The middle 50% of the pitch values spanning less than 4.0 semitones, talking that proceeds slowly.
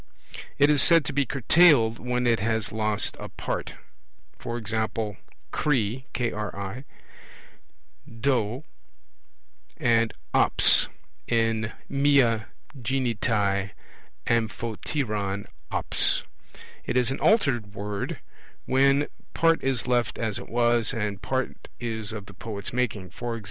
Yes: average, 3.5 semitones; slow, 105 wpm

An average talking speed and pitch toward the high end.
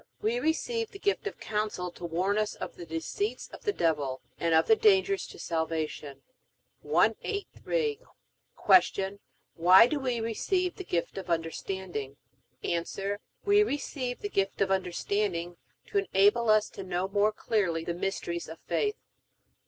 Yes: average, 150 wpm; high, 200 Hz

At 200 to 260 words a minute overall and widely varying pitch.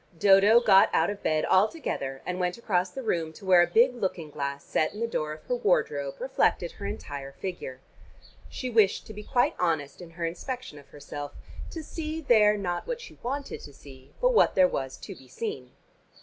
Yes: fast, 205 wpm; wide, 7.6 semitones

